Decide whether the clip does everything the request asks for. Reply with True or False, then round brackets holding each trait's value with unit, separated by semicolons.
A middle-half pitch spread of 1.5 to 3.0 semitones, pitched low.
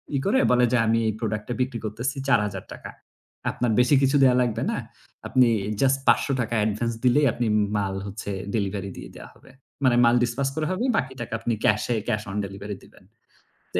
False (3.4 semitones; 120 Hz)